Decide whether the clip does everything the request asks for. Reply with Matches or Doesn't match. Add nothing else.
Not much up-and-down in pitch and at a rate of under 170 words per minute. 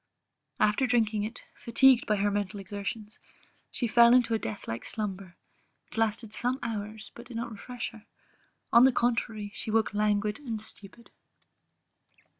Matches